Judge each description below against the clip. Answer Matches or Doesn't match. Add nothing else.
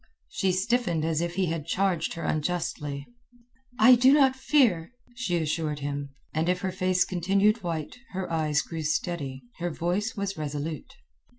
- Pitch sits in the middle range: Matches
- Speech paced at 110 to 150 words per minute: Doesn't match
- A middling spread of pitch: Matches